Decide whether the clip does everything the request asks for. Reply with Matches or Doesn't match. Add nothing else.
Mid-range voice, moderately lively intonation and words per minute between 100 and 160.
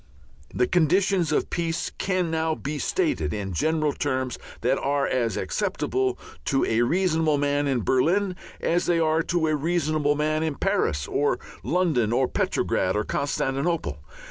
Matches